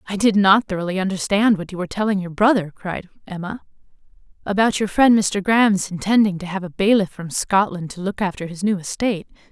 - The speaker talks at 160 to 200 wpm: Yes, average, 195 wpm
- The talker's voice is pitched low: No, high, 195 Hz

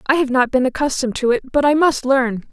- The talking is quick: Yes, fast, 260 wpm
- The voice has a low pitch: No, very high, 265 Hz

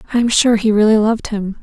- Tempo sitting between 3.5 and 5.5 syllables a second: No, 6.7 syllables/s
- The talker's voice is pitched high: Yes, high, 220 Hz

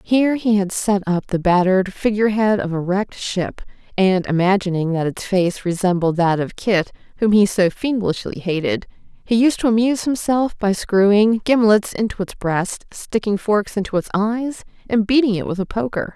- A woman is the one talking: Yes, female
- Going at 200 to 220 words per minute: No, average, 180 wpm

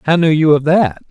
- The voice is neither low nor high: Yes, medium, 155 Hz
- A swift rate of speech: Yes, fast, 270 wpm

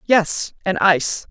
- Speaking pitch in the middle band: Yes, medium, 180 Hz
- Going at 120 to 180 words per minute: Yes, average, 140 wpm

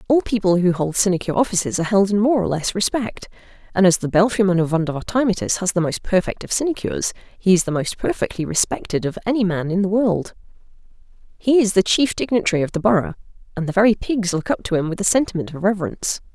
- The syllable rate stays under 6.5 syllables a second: No, 6.6 syllables/s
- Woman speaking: Yes, female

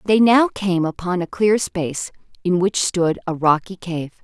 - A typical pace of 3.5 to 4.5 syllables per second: Yes, 4.4 syllables/s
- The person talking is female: Yes, female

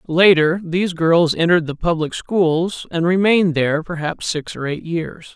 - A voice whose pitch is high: No, medium, 170 Hz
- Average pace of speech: Yes, average, 170 wpm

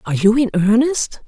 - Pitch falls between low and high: No, high, 230 Hz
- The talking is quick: No, average, 190 wpm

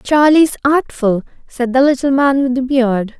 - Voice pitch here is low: No, very high, 265 Hz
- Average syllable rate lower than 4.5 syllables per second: Yes, 4.2 syllables/s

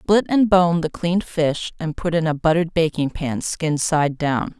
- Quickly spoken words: Yes, fast, 210 wpm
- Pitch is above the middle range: No, medium, 165 Hz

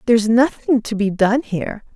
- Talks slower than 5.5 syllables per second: Yes, 5.2 syllables/s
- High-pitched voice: Yes, high, 225 Hz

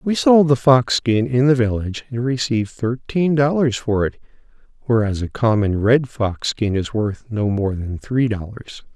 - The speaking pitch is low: Yes, low, 120 Hz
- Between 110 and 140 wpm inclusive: No, average, 180 wpm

